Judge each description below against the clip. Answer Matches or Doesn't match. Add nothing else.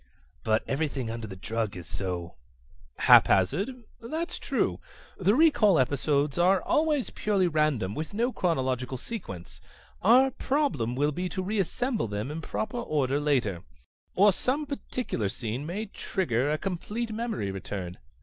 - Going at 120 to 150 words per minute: Matches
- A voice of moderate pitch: Matches